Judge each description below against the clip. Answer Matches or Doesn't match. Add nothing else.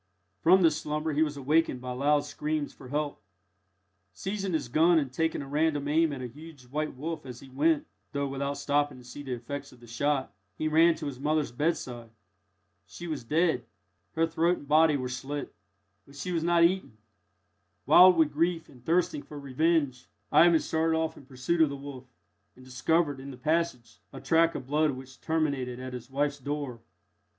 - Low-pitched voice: Doesn't match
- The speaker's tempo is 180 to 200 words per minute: Matches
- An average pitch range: Matches